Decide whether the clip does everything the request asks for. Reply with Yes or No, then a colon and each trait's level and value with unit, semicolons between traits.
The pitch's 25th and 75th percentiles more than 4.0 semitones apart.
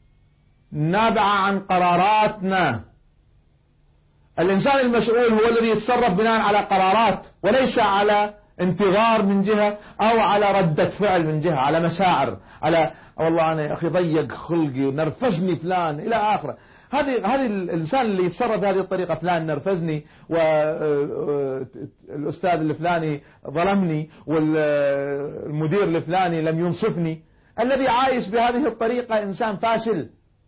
Yes: average, 5.3 semitones